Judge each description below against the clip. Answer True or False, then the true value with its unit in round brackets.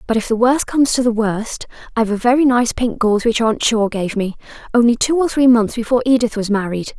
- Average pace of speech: False (240 wpm)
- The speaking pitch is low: False (230 Hz)